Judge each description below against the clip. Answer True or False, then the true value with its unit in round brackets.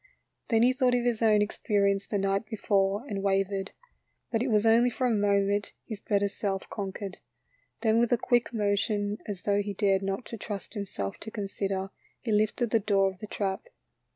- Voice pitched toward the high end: True (205 Hz)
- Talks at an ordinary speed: True (185 wpm)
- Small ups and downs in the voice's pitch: True (2.2 semitones)